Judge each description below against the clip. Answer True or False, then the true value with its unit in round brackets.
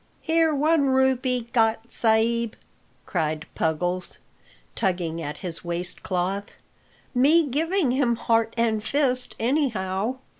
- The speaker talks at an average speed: False (110 wpm)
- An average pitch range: False (6.1 semitones)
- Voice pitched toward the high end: True (230 Hz)